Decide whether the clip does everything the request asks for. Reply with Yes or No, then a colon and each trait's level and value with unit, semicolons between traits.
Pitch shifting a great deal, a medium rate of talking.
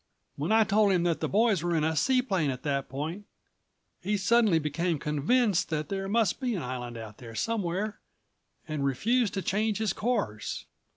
Yes: wide, 6.2 semitones; average, 180 wpm